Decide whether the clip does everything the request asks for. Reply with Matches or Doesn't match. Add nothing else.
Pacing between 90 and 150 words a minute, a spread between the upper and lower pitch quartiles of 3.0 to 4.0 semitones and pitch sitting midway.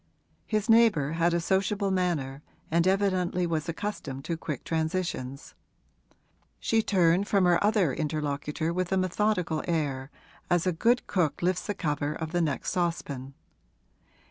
Matches